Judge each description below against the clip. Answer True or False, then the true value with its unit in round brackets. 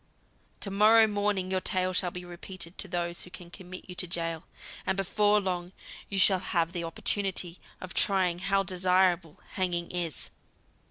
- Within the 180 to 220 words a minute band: False (165 wpm)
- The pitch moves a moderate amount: False (1.8 semitones)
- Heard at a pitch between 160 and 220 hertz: True (185 Hz)